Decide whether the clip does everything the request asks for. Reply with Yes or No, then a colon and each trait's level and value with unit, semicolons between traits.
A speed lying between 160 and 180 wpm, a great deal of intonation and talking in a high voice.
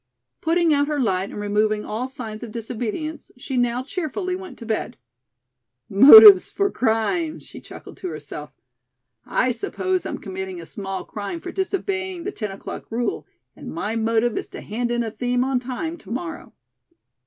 Yes: average, 170 wpm; wide, 7.3 semitones; high, 245 Hz